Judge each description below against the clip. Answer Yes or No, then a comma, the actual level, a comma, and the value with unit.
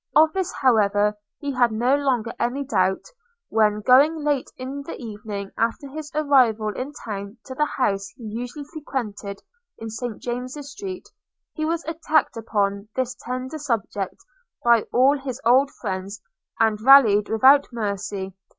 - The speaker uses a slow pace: No, average, 150 wpm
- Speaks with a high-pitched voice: Yes, high, 245 Hz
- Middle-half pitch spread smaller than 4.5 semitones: No, average, 5.0 semitones